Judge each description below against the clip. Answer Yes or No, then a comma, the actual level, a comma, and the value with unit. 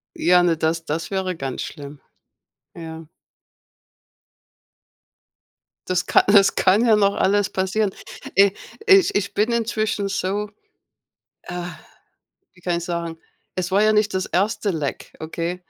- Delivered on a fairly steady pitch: No, average, 3.4 semitones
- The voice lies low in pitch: No, medium, 185 Hz